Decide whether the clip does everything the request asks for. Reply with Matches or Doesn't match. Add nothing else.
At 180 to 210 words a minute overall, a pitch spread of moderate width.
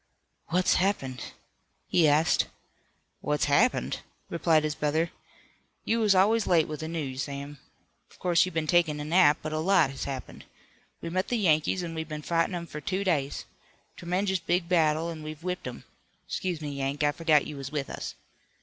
Matches